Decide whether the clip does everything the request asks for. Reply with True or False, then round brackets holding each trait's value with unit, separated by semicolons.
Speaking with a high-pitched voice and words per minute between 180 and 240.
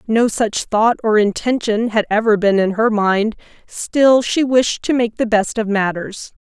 True (220 Hz; 185 wpm)